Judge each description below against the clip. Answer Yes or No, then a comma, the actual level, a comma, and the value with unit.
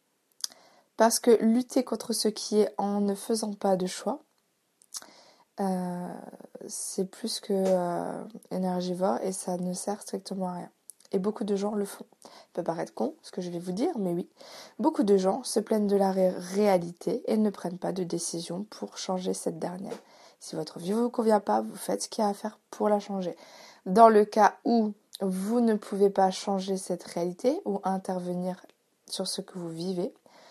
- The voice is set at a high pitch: Yes, high, 200 Hz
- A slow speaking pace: No, average, 195 wpm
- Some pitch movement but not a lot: Yes, average, 3.0 semitones